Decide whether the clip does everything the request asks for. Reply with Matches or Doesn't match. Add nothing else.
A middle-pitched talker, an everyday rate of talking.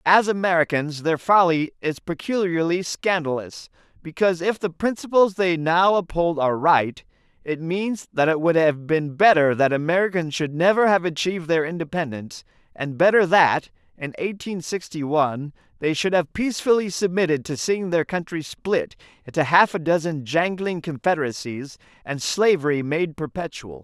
Matches